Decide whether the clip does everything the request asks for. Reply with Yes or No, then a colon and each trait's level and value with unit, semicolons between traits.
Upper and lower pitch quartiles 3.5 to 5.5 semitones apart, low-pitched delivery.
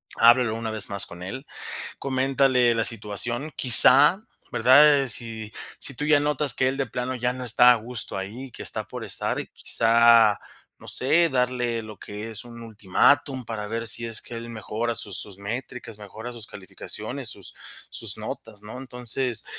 No: average, 2.9 semitones; low, 120 Hz